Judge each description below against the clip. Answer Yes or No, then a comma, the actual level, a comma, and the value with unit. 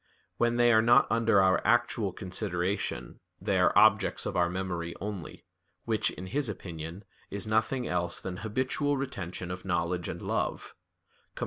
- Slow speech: No, average, 155 wpm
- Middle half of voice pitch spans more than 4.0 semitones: Yes, average, 4.5 semitones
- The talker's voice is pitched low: Yes, low, 100 Hz